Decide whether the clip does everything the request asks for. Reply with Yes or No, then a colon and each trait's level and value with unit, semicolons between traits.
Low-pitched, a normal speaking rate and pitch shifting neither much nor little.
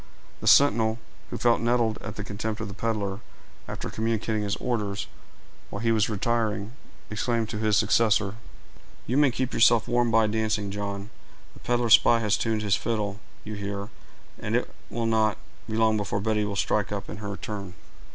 No: low, 110 Hz; average, 180 wpm; narrow, 2.0 semitones